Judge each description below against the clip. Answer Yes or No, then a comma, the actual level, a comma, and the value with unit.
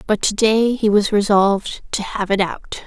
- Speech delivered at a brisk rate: No, average, 190 wpm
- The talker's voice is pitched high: Yes, high, 205 Hz